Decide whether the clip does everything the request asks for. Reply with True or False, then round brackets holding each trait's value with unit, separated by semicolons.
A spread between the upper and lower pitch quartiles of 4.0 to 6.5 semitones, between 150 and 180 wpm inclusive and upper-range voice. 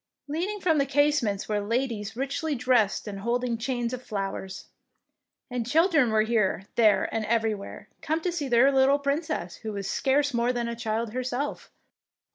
True (4.3 semitones; 165 wpm; 245 Hz)